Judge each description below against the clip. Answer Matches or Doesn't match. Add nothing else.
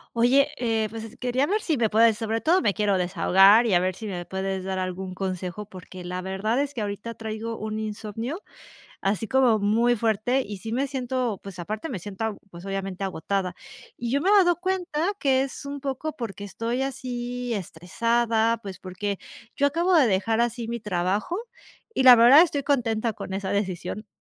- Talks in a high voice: Matches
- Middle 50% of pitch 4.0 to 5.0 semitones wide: Matches